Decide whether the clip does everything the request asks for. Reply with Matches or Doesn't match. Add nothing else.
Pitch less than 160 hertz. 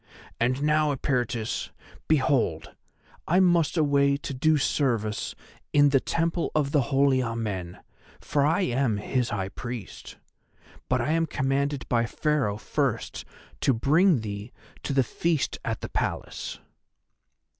Matches